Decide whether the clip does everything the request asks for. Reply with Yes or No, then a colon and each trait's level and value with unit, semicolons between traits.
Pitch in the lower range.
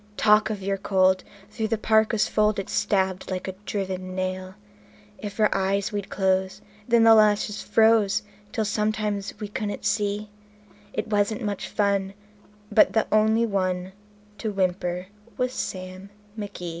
No: high, 205 Hz